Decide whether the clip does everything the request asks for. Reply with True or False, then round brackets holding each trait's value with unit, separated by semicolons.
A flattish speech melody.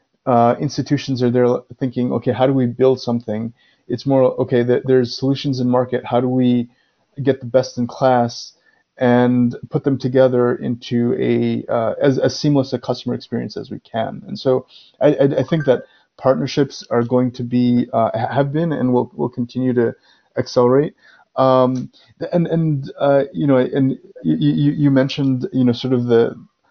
True (1.8 semitones)